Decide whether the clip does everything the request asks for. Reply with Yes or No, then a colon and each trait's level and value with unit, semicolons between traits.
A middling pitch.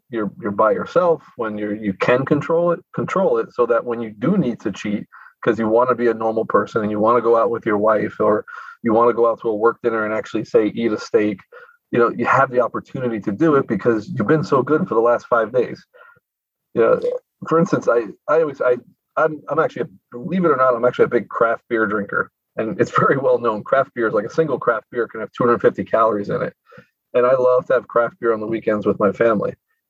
No: low, 125 Hz